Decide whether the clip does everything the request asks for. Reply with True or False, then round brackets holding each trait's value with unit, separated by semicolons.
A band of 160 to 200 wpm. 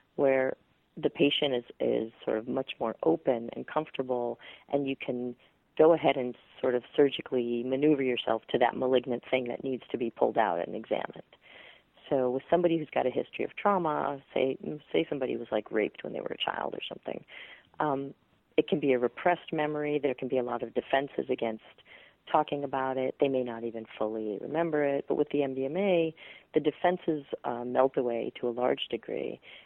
True (190 wpm)